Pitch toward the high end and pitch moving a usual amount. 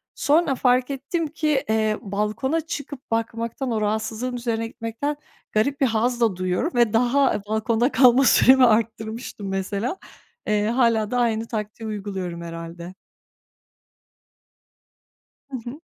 Yes: high, 230 Hz; average, 3.4 semitones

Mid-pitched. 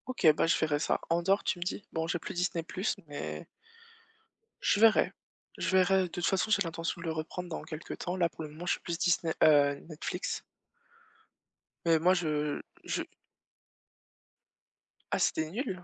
Yes: medium, 170 Hz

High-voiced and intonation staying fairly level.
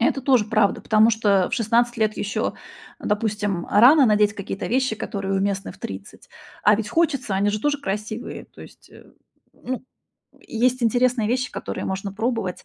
No: high, 220 Hz; average, 3.3 semitones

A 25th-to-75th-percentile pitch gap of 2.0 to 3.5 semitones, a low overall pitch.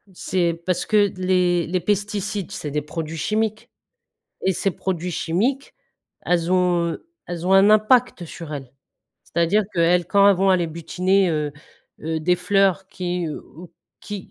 No: average, 2.8 semitones; medium, 180 Hz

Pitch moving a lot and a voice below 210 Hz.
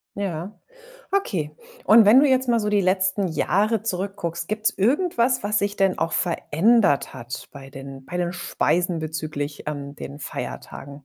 Yes: wide, 5.7 semitones; medium, 185 Hz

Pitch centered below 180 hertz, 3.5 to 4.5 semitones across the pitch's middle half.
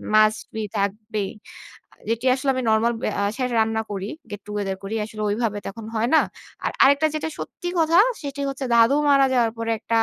No: high, 225 Hz; average, 3.8 semitones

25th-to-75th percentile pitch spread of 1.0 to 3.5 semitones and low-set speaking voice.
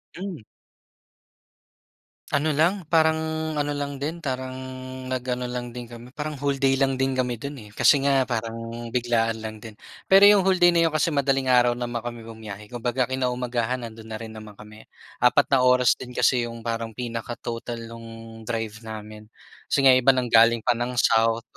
Yes: average, 3.0 semitones; low, 125 Hz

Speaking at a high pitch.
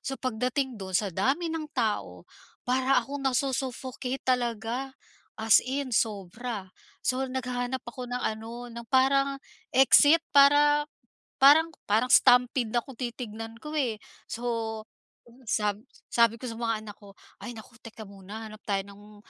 Yes: high, 245 Hz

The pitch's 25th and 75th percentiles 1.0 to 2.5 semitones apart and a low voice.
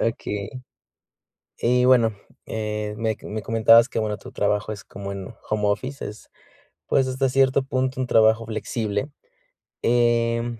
No: average, 2.9 semitones; low, 115 Hz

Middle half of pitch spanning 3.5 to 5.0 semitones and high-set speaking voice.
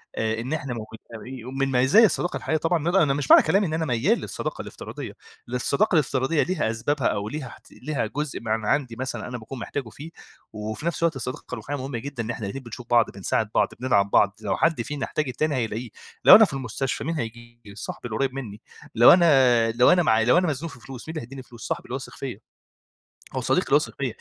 No: average, 4.6 semitones; low, 130 Hz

